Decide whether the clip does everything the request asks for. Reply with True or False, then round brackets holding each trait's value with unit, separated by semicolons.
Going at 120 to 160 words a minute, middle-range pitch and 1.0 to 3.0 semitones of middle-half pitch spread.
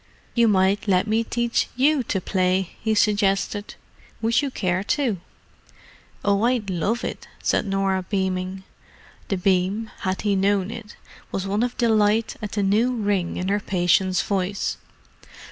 False (150 wpm; 200 Hz; 2.7 semitones)